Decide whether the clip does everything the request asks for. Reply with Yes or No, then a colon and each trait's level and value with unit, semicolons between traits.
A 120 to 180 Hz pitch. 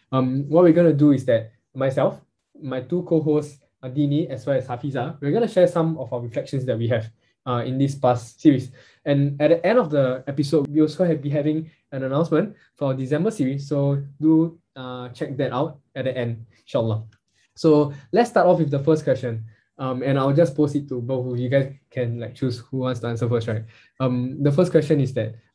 Yes: medium, 140 Hz